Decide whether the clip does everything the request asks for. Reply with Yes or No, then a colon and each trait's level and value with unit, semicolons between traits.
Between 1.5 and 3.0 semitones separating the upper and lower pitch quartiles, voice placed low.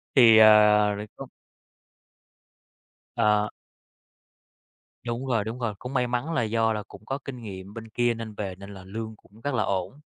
Yes: narrow, 2.5 semitones; low, 110 Hz